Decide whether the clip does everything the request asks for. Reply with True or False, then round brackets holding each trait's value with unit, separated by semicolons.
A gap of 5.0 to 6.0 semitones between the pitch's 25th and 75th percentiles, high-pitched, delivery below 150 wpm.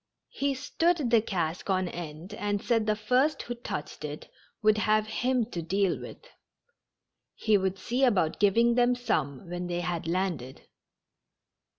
False (5.3 semitones; 205 Hz; 155 wpm)